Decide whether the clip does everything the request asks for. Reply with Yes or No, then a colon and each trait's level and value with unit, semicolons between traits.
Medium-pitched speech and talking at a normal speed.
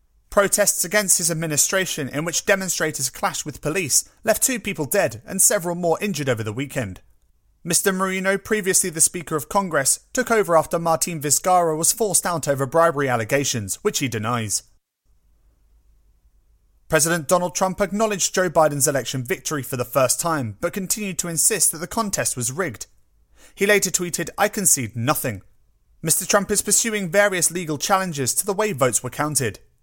Yes: medium, 170 Hz; average, 165 wpm